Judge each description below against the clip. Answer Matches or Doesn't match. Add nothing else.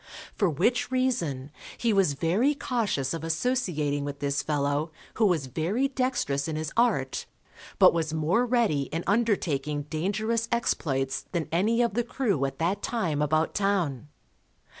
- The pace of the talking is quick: Doesn't match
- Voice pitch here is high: Doesn't match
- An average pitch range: Doesn't match